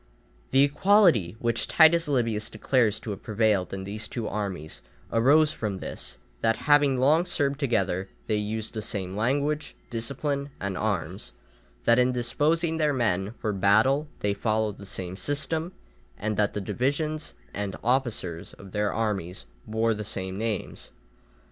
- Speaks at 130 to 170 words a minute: Yes, average, 150 wpm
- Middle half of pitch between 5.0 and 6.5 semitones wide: Yes, wide, 5.6 semitones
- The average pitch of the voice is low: Yes, low, 110 Hz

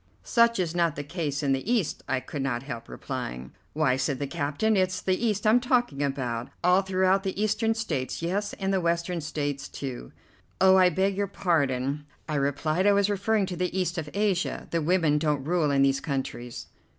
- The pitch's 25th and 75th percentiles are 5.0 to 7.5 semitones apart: Yes, wide, 5.5 semitones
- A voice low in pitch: No, medium, 170 Hz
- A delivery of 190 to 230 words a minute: Yes, average, 200 wpm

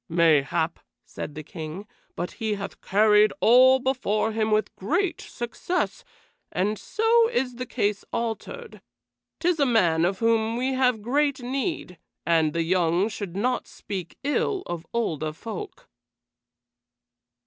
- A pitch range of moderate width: No, wide, 6.5 semitones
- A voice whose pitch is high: Yes, high, 220 Hz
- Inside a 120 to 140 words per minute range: Yes, slow, 135 wpm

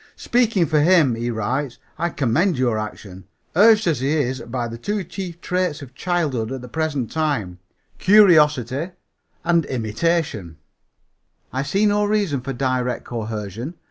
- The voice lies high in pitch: No, medium, 140 Hz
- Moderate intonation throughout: No, wide, 6.5 semitones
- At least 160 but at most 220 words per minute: No, average, 145 wpm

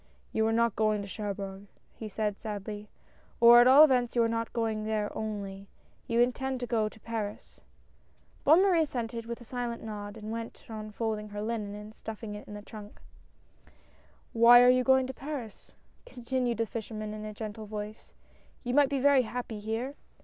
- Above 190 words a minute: Yes, average, 200 wpm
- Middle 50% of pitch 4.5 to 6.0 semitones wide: No, narrow, 2.4 semitones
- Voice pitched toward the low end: No, high, 225 Hz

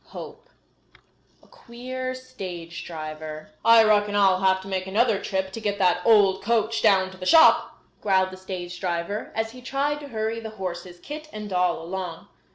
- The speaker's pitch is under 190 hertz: No, high, 195 Hz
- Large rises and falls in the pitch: No, average, 3.8 semitones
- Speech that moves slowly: No, average, 180 wpm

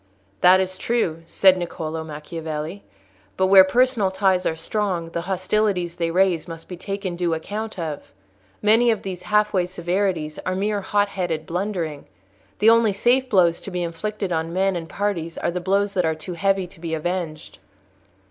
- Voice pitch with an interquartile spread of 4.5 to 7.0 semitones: No, average, 3.2 semitones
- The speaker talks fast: No, average, 175 wpm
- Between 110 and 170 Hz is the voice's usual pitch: No, medium, 185 Hz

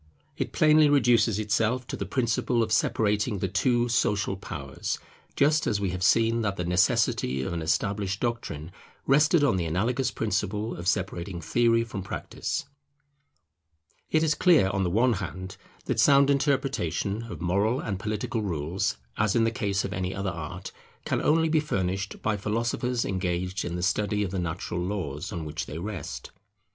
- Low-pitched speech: Yes, low, 100 Hz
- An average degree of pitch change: Yes, average, 4.4 semitones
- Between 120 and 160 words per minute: No, average, 170 wpm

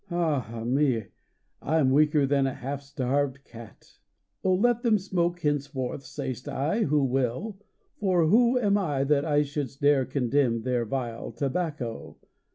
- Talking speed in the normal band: Yes, average, 155 wpm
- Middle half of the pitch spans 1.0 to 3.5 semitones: No, average, 4.0 semitones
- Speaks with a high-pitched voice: No, medium, 140 Hz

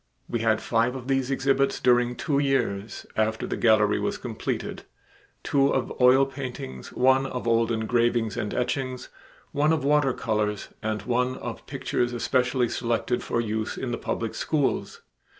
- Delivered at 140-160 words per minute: Yes, average, 155 wpm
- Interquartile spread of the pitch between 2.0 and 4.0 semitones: Yes, average, 2.9 semitones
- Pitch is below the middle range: Yes, low, 125 Hz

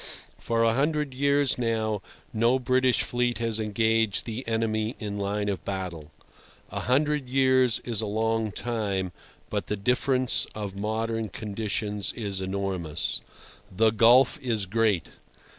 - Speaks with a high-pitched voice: No, low, 115 Hz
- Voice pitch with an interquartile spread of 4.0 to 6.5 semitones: No, average, 3.2 semitones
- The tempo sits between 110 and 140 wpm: Yes, slow, 135 wpm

